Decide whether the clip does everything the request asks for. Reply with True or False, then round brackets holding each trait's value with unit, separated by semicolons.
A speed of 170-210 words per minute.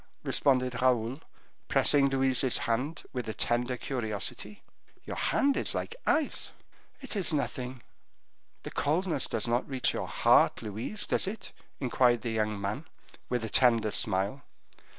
False (140 wpm)